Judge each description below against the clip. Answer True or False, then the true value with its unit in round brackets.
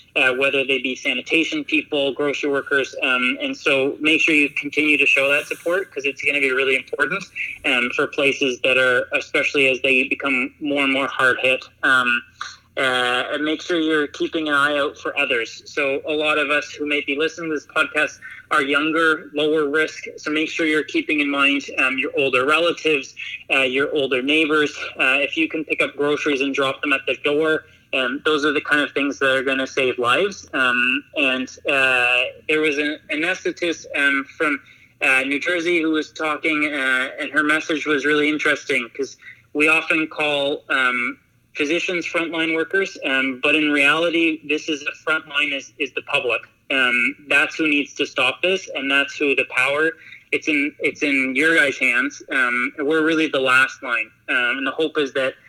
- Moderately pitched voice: True (150 Hz)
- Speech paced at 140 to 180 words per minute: False (195 wpm)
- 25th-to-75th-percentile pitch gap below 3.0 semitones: True (2.6 semitones)